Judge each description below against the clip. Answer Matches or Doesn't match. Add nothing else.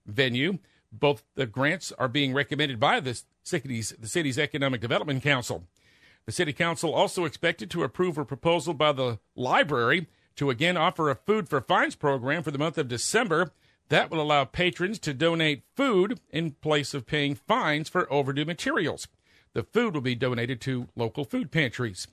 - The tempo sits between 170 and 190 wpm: Matches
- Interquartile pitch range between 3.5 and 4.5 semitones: Matches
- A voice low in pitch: Doesn't match